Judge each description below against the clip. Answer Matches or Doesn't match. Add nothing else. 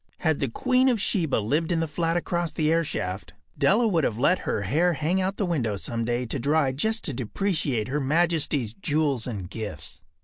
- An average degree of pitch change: Doesn't match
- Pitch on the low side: Doesn't match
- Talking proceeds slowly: Doesn't match